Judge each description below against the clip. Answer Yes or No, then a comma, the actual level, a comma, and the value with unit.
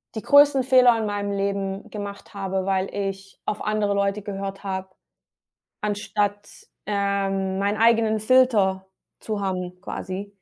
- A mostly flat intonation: Yes, narrow, 1.6 semitones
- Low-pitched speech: No, high, 200 Hz